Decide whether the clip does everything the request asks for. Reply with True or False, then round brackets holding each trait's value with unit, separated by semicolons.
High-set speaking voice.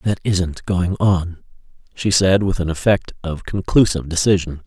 False (90 Hz)